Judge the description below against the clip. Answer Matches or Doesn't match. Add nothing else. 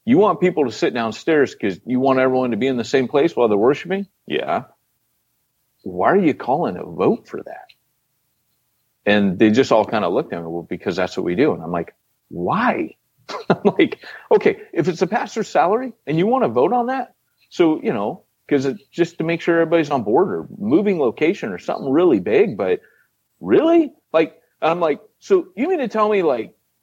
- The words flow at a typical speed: Doesn't match